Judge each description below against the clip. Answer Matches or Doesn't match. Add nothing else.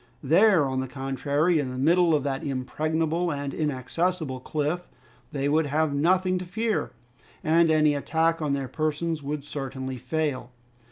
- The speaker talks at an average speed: Matches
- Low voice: Doesn't match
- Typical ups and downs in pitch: Matches